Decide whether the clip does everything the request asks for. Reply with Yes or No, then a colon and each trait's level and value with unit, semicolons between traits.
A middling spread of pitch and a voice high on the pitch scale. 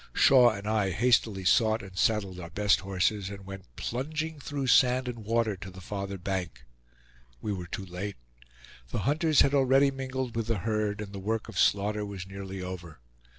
No: average, 4.2 semitones; low, 105 Hz